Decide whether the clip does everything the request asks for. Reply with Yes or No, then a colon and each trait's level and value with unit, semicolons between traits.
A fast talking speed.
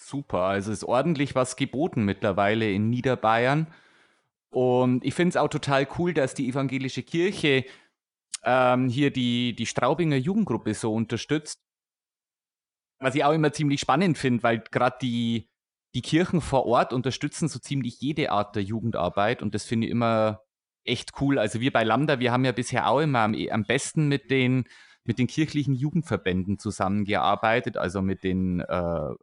No: average, 165 wpm